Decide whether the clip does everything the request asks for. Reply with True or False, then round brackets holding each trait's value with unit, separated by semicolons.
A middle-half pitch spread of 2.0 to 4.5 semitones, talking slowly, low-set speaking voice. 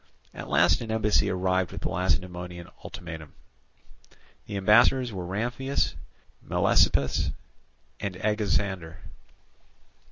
True (3.4 semitones; 95 wpm; 95 Hz)